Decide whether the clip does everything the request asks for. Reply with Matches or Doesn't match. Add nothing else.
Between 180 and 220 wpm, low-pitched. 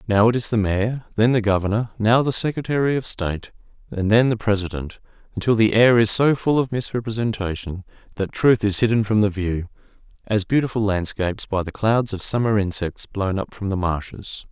Matches